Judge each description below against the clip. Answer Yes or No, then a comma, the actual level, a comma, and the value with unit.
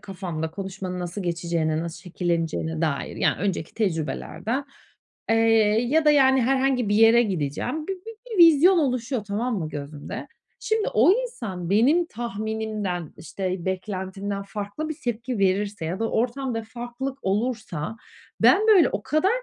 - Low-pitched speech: No, high, 210 Hz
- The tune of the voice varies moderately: No, wide, 6.5 semitones